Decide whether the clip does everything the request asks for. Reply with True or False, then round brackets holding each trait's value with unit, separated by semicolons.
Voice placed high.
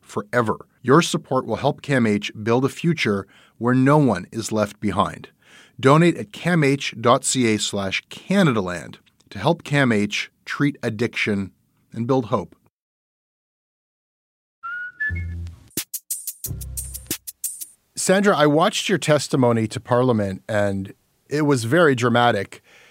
False (125 Hz)